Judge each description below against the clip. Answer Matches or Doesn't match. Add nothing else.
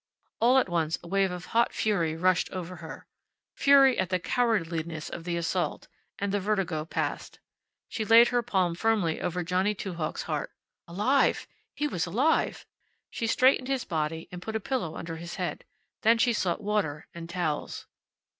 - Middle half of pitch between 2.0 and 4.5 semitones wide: Doesn't match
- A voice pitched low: Doesn't match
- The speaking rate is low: Doesn't match